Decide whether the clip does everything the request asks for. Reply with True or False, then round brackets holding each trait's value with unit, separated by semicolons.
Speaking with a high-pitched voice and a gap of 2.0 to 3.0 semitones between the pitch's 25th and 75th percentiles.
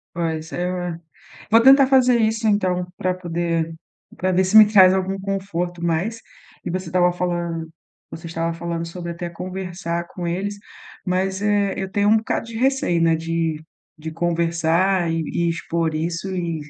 False (175 Hz; 2.4 semitones)